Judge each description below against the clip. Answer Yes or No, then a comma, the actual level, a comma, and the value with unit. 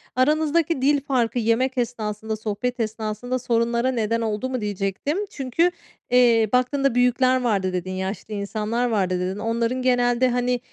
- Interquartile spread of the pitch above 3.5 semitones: No, average, 3.1 semitones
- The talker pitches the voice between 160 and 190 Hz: No, high, 235 Hz